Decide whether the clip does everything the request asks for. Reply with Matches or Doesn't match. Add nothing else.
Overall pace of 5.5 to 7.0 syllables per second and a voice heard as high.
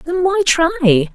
Doesn't match